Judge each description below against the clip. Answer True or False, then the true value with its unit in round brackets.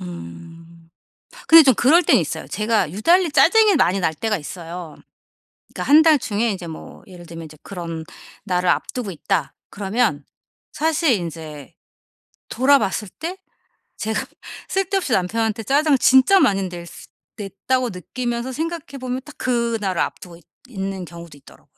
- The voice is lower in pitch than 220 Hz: True (210 Hz)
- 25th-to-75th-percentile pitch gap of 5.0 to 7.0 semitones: False (7.4 semitones)